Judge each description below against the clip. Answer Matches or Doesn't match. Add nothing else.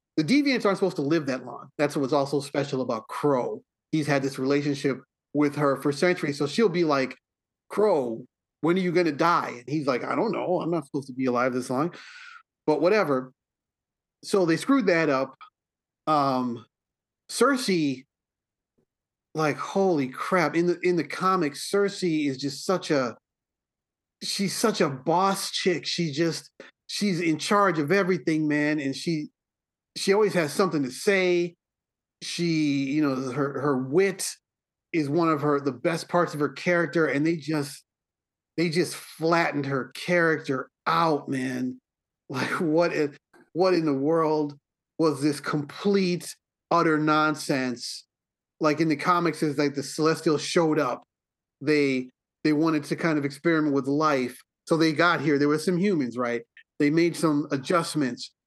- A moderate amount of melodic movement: Matches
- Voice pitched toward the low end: Doesn't match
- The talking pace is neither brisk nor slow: Matches